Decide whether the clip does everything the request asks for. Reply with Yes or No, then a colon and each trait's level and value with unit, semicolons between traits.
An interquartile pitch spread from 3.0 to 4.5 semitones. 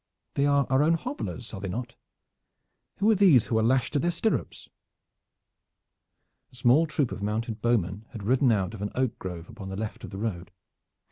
No: wide, 5.4 semitones